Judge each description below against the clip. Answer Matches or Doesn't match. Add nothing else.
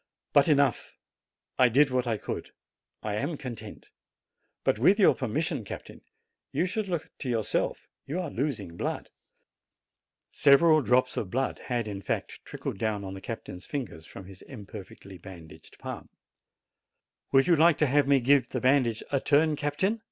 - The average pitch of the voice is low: Matches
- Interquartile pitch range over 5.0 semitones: Matches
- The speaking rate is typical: Matches